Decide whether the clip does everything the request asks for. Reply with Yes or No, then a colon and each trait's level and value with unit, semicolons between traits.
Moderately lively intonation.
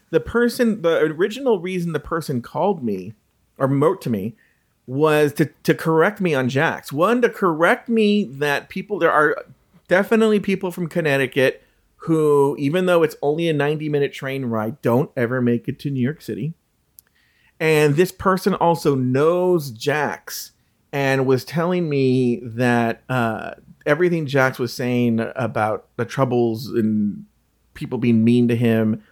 No: wide, 6.0 semitones